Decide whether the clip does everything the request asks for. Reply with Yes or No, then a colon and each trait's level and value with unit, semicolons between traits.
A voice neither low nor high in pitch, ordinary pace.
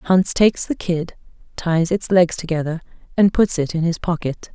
Yes: medium, 175 Hz; average, 185 wpm